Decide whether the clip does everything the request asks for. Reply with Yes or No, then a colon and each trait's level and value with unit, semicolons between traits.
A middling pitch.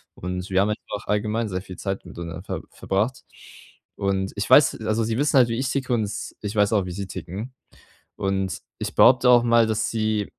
No: low, 105 Hz